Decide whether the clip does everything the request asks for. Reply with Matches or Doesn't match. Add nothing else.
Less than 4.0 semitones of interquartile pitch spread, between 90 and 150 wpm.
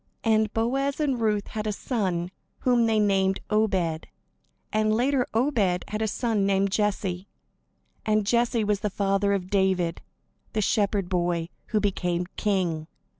Matches